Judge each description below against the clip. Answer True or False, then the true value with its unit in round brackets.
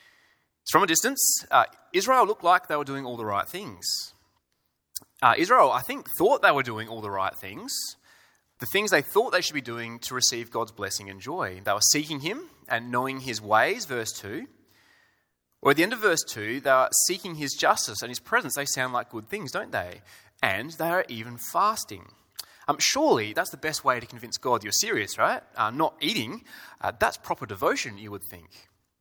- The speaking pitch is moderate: False (125 Hz)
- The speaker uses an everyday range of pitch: False (6.1 semitones)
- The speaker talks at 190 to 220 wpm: True (205 wpm)